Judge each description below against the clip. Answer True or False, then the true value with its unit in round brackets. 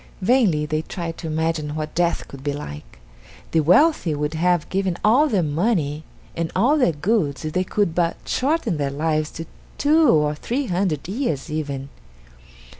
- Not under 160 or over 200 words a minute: True (170 wpm)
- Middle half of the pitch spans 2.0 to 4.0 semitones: False (5.0 semitones)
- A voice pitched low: False (165 Hz)